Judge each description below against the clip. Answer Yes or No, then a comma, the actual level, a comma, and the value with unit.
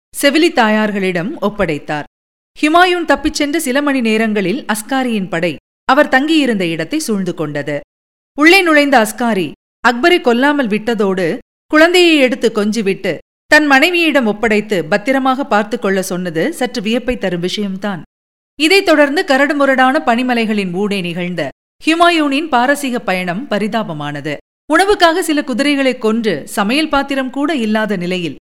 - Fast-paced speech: No, average, 115 wpm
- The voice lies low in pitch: No, high, 240 Hz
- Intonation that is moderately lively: No, wide, 6.1 semitones